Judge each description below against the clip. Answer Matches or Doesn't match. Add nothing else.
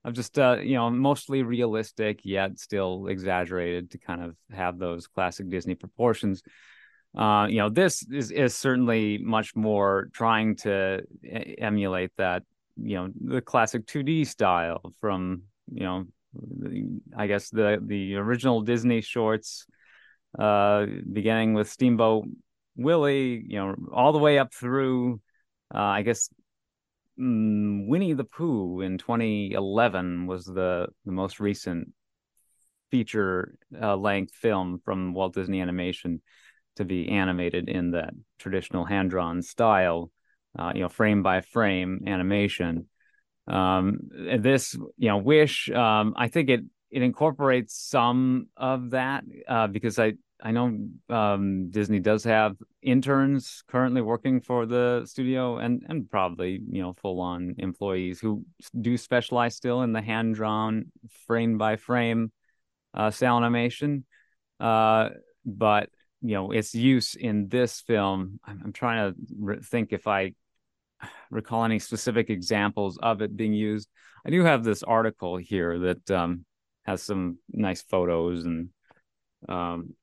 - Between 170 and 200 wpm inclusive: Doesn't match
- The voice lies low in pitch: Matches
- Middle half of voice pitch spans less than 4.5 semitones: Matches